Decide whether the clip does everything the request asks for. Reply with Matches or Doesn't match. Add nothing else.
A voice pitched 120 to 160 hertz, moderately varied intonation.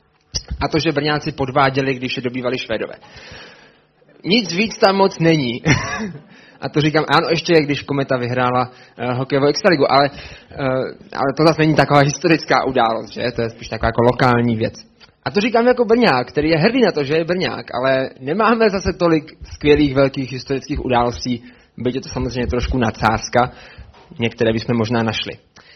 Matches